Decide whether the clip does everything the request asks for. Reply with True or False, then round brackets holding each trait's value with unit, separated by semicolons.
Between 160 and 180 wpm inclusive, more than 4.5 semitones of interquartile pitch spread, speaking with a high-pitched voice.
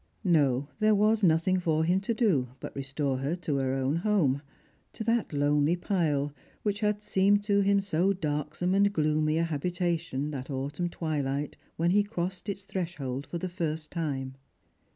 False (175 wpm; 5.1 semitones; 165 Hz)